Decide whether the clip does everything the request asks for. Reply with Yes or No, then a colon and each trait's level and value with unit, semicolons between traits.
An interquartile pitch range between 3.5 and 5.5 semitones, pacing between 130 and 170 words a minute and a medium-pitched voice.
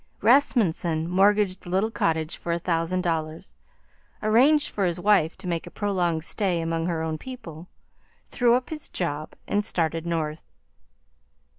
Yes: average, 4.1 semitones; average, 150 wpm; medium, 175 Hz